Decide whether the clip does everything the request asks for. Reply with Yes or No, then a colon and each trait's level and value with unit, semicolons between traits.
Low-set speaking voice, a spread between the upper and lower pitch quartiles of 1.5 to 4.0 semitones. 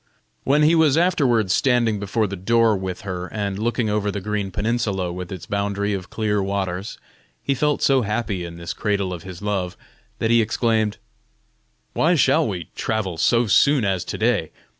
Yes: low, 105 Hz; average, 3.6 semitones